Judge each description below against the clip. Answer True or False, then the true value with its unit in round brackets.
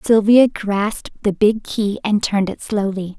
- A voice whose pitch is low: False (210 Hz)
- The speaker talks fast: False (170 wpm)